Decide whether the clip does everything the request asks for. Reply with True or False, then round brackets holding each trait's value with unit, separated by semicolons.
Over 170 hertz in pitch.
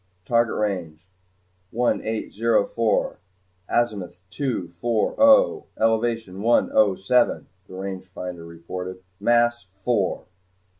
False (105 Hz)